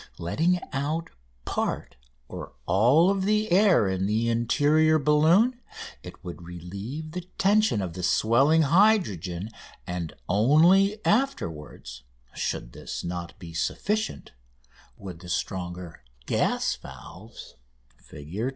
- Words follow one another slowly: Yes, slow, 115 wpm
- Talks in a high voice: No, low, 120 Hz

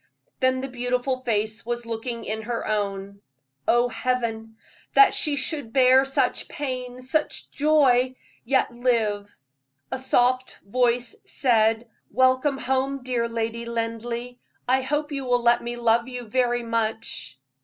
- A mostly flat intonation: Yes, narrow, 2.1 semitones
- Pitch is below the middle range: No, high, 245 Hz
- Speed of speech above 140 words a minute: No, slow, 135 wpm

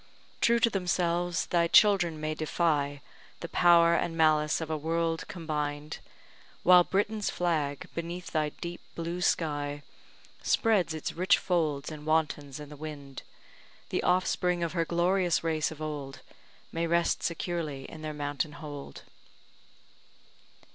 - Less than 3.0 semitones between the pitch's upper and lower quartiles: Yes, narrow, 2.5 semitones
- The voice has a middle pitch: Yes, medium, 165 Hz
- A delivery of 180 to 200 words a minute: No, slow, 135 wpm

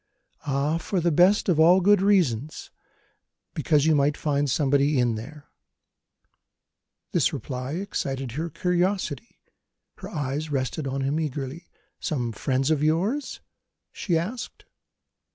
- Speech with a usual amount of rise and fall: Yes, average, 4.1 semitones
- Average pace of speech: No, slow, 125 wpm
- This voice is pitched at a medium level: Yes, medium, 150 Hz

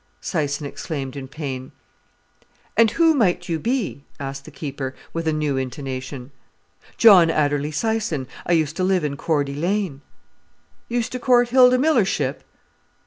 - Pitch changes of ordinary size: No, wide, 7.4 semitones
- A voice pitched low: No, medium, 155 Hz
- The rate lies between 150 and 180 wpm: No, average, 140 wpm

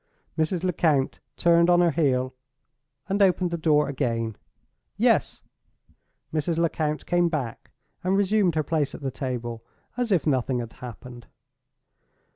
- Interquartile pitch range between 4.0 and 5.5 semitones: Yes, average, 5.2 semitones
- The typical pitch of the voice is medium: Yes, medium, 155 Hz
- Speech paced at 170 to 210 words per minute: No, slow, 135 wpm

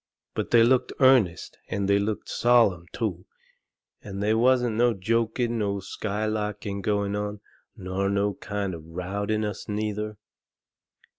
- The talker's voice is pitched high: No, low, 105 Hz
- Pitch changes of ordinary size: No, narrow, 2.1 semitones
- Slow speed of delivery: Yes, slow, 130 wpm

